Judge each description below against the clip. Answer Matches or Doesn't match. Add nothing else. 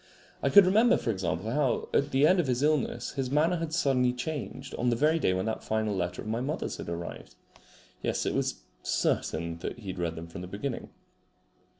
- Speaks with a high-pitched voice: Doesn't match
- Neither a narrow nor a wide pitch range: Doesn't match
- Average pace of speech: Doesn't match